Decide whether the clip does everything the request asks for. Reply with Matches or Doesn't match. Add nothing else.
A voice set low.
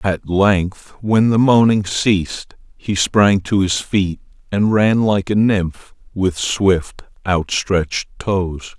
Matches